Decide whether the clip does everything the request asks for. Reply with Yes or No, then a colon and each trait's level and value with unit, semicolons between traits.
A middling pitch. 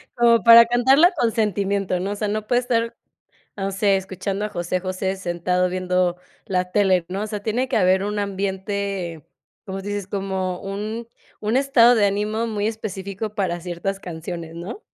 No: high, 200 Hz